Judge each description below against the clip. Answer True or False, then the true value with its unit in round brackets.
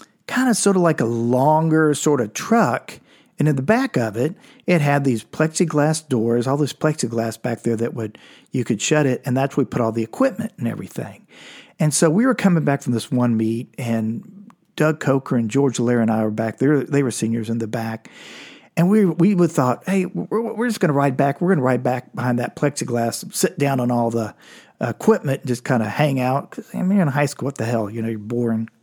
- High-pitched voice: False (140 Hz)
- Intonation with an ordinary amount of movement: False (6.6 semitones)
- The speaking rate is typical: False (245 wpm)